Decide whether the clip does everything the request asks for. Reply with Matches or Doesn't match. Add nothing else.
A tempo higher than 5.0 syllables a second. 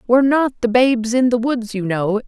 Matches